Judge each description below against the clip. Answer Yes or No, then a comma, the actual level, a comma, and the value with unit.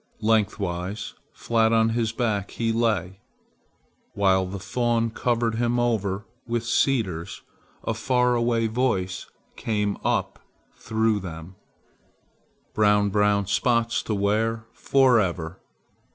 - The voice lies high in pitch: No, low, 110 Hz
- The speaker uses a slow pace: Yes, slow, 110 wpm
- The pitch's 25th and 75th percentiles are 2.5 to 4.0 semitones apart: Yes, average, 2.9 semitones